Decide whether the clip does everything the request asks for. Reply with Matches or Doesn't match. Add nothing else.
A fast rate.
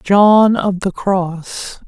Doesn't match